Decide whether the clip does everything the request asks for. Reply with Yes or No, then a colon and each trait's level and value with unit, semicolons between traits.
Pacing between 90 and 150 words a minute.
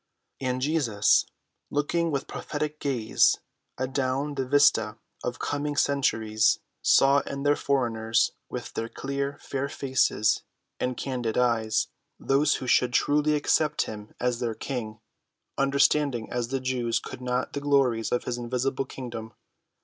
Yes: slow, 135 wpm